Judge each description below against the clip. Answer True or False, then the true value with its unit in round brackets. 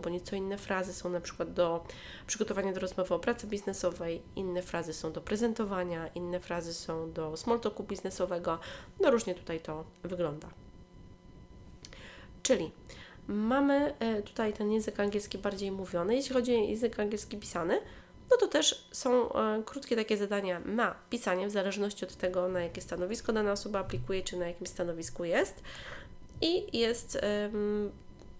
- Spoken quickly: False (150 wpm)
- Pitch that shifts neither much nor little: True (3.5 semitones)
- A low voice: False (195 Hz)